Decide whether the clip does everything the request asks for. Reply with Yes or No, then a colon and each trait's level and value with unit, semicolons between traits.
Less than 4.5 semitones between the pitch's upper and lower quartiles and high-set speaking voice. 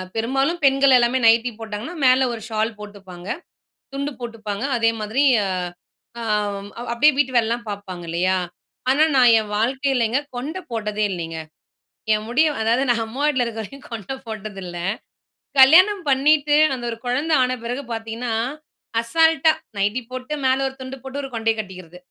Yes: average, 4.0 semitones; high, 235 Hz